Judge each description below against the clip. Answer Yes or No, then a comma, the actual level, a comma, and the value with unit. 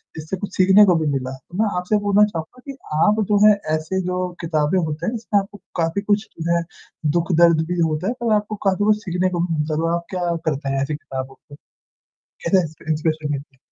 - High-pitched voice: No, medium, 170 Hz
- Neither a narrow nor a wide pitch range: Yes, average, 4.3 semitones